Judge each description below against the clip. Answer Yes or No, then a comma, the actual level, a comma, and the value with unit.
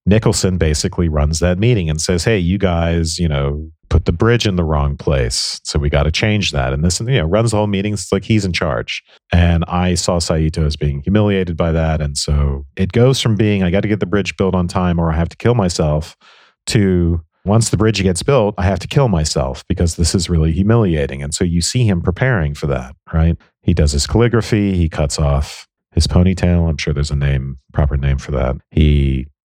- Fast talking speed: Yes, fast, 225 wpm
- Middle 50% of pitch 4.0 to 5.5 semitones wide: Yes, average, 4.3 semitones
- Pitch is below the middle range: Yes, very low, 85 Hz